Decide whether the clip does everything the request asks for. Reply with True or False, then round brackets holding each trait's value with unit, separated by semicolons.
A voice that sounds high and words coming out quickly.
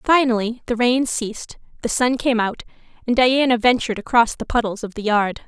False (235 Hz; 185 wpm)